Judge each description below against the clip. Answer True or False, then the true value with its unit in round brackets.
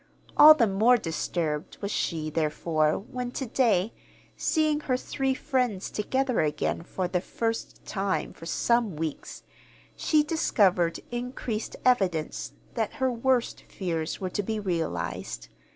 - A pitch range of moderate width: False (6.9 semitones)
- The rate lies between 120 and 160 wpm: True (135 wpm)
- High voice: True (210 Hz)